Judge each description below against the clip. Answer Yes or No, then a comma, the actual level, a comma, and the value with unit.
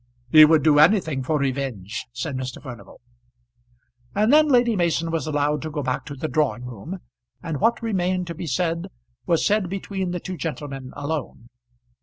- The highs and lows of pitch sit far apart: No, average, 4.9 semitones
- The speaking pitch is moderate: Yes, medium, 155 Hz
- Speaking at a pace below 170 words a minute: No, average, 175 wpm